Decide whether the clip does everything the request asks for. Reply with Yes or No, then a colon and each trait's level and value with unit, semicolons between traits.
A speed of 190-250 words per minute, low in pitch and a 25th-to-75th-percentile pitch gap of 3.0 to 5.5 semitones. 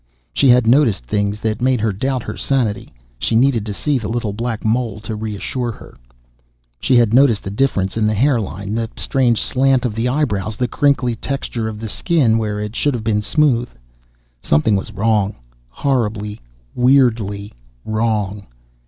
No: average, 170 wpm; low, 115 Hz; average, 3.3 semitones